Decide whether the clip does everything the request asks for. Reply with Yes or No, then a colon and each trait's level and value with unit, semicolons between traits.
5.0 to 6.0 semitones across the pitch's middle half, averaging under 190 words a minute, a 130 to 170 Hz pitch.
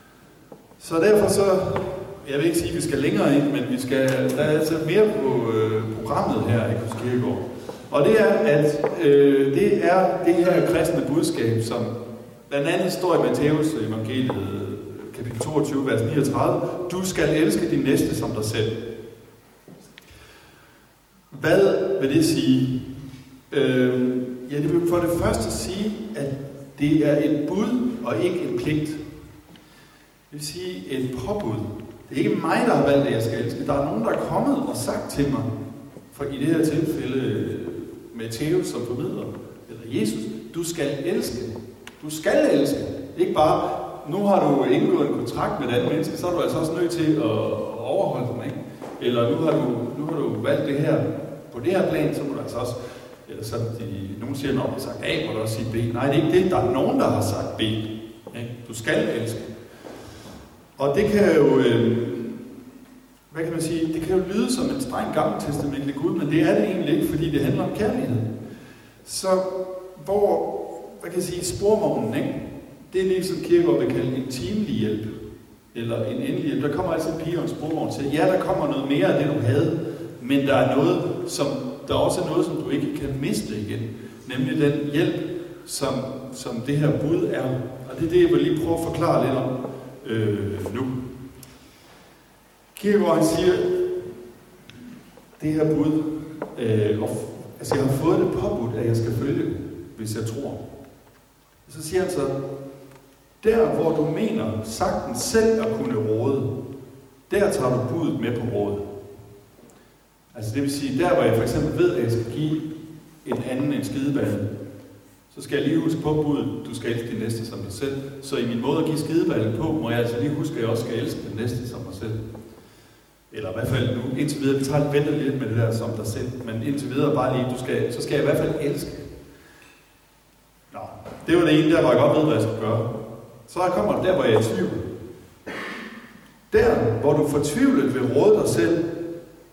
No: wide, 5.4 semitones; average, 195 wpm; medium, 140 Hz